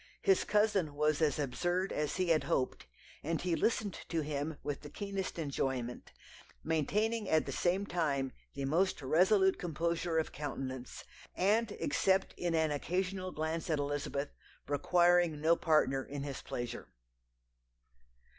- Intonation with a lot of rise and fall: No, average, 4.2 semitones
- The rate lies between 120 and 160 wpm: Yes, average, 140 wpm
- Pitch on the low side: No, medium, 160 Hz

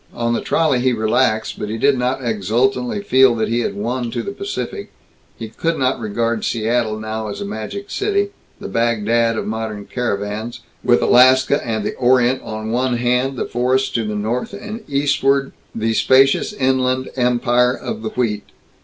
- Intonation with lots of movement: No, average, 2.8 semitones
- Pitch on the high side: No, low, 120 Hz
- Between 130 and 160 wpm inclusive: No, average, 175 wpm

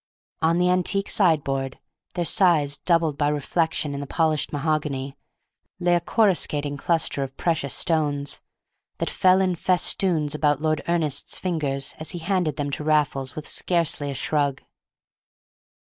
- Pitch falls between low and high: Yes, medium, 155 Hz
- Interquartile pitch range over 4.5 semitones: No, average, 3.3 semitones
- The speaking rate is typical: Yes, average, 145 wpm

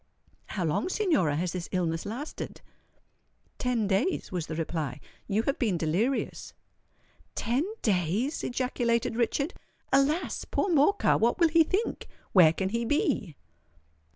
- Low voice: No, high, 230 Hz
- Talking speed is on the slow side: Yes, slow, 125 wpm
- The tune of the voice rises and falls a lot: Yes, wide, 8.2 semitones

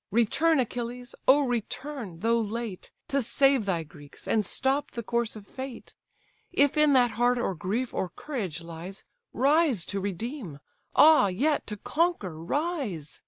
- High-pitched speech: Yes, high, 235 Hz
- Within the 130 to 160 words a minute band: Yes, average, 150 wpm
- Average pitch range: No, wide, 5.9 semitones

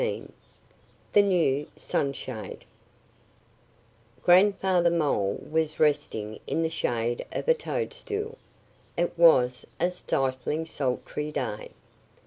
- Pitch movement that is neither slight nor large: No, wide, 5.7 semitones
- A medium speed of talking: No, slow, 100 wpm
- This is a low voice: No, medium, 160 Hz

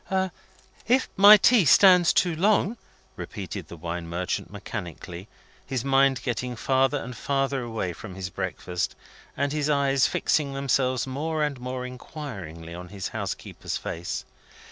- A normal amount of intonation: No, wide, 7.6 semitones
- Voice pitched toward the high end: No, low, 130 Hz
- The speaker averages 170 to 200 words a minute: No, average, 140 wpm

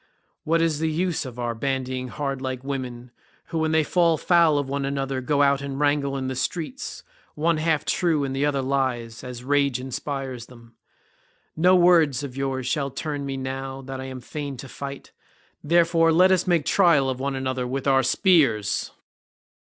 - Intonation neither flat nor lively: Yes, average, 3.2 semitones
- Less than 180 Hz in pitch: Yes, medium, 140 Hz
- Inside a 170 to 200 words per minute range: Yes, average, 180 wpm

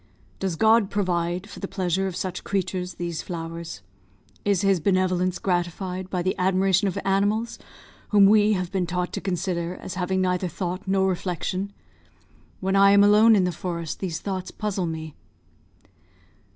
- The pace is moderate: Yes, average, 160 wpm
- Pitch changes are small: Yes, narrow, 1.8 semitones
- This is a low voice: No, medium, 185 Hz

